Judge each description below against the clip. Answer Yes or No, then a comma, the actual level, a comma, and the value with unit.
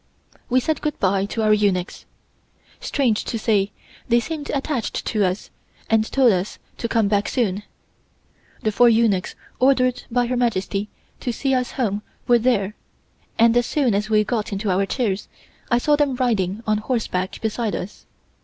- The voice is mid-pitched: No, high, 225 Hz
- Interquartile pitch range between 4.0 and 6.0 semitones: No, average, 3.5 semitones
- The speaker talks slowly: No, average, 170 wpm